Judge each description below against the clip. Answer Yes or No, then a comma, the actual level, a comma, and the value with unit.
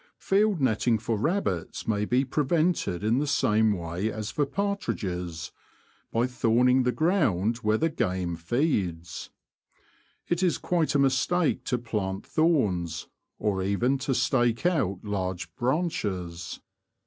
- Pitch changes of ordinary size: No, wide, 7.4 semitones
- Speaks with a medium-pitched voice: No, low, 115 Hz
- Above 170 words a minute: No, slow, 135 wpm